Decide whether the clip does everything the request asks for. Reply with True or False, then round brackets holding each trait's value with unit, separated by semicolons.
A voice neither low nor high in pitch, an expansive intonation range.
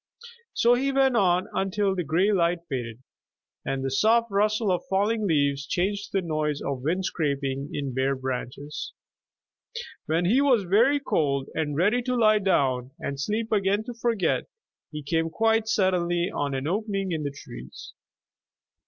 True (180 Hz; 7.0 semitones)